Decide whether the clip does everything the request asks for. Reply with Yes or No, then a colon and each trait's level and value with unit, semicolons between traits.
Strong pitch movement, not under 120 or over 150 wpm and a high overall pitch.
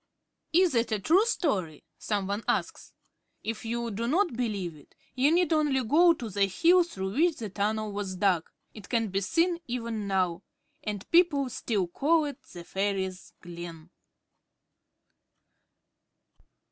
Yes: wide, 7.5 semitones; average, 145 wpm; high, 220 Hz